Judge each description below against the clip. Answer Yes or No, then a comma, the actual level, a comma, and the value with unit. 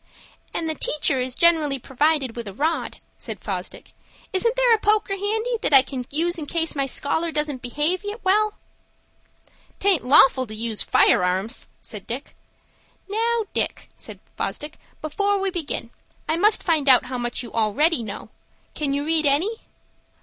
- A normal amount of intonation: No, wide, 6.5 semitones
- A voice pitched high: Yes, very high, 300 Hz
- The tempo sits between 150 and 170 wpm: Yes, average, 165 wpm